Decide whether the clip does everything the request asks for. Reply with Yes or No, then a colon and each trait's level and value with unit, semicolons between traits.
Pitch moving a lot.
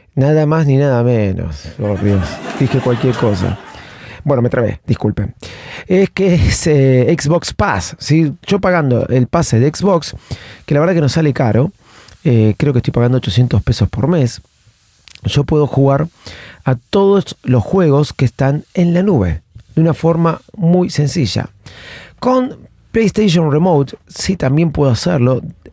Yes: wide, 5.7 semitones